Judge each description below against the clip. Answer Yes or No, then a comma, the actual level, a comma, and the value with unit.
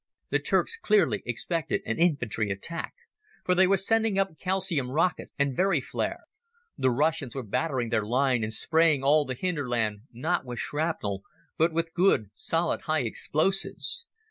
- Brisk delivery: No, average, 155 wpm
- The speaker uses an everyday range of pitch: No, wide, 6.3 semitones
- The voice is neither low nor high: Yes, medium, 155 Hz